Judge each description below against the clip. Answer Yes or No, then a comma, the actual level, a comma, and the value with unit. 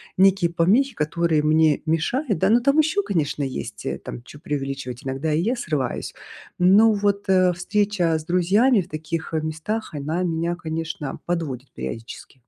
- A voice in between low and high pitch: Yes, medium, 165 Hz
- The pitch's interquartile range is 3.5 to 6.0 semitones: Yes, average, 4.8 semitones